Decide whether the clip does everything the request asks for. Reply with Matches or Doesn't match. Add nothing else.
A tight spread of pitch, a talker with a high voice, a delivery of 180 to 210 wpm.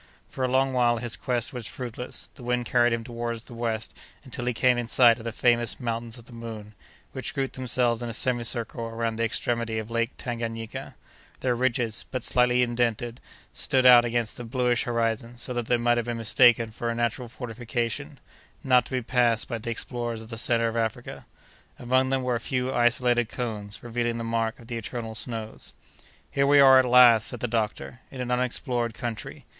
Doesn't match